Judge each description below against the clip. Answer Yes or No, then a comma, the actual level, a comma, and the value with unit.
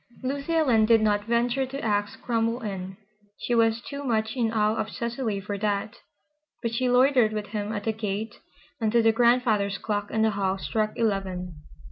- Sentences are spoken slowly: No, average, 180 wpm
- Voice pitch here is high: Yes, high, 220 Hz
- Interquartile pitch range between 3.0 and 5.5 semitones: No, narrow, 2.5 semitones